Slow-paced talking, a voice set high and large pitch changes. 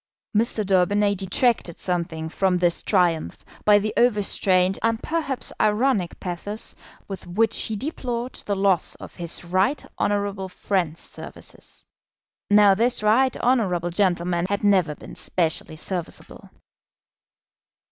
No: slow, 120 wpm; high, 195 Hz; average, 3.3 semitones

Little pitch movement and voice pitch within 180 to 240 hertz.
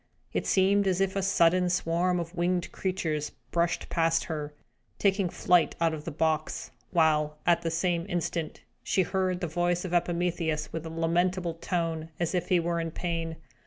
No: narrow, 1.7 semitones; medium, 170 Hz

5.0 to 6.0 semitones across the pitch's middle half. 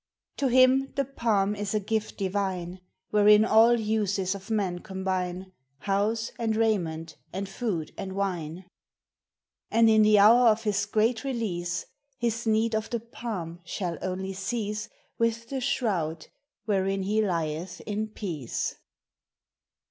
No: average, 3.1 semitones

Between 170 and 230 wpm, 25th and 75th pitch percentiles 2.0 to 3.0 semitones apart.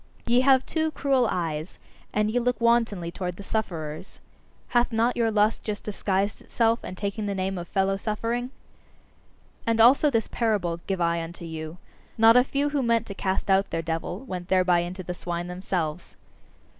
No: average, 180 wpm; average, 4.8 semitones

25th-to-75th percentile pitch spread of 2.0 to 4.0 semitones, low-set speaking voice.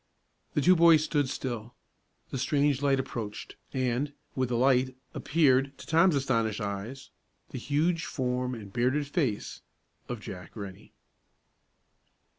Yes: average, 3.4 semitones; low, 130 Hz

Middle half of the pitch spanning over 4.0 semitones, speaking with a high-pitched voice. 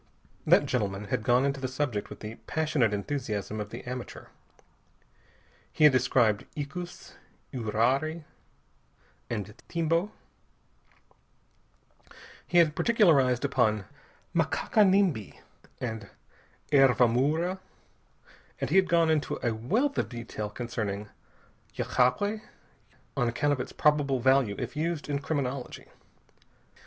No: wide, 5.4 semitones; low, 130 Hz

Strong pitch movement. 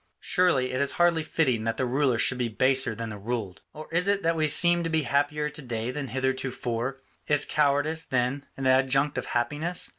No: average, 3.7 semitones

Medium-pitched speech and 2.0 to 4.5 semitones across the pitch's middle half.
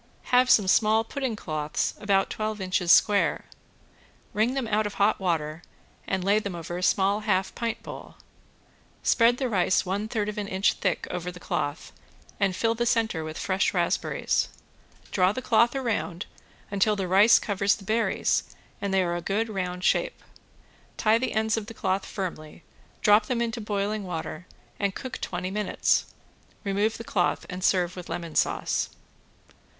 No: high, 200 Hz; average, 3.2 semitones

